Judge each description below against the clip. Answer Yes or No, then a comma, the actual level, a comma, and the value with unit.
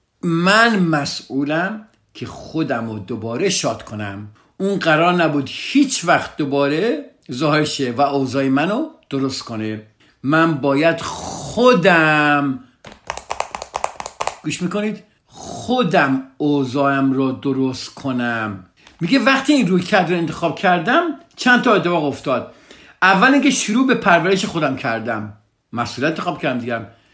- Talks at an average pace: Yes, average, 115 wpm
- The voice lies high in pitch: No, medium, 155 Hz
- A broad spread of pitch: Yes, wide, 6.6 semitones